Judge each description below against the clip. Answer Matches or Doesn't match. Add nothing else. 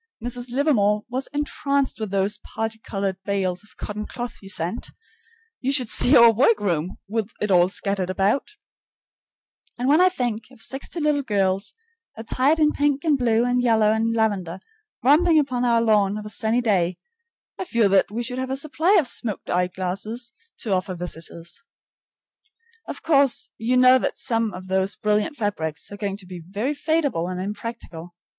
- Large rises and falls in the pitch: Doesn't match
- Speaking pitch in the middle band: Doesn't match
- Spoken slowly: Doesn't match